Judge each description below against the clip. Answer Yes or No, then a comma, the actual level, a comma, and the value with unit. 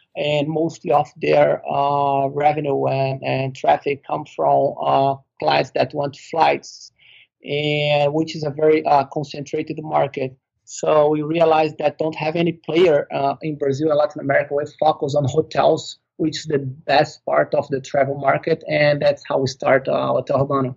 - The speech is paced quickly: No, average, 170 wpm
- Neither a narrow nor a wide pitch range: No, narrow, 2.1 semitones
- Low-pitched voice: No, medium, 145 Hz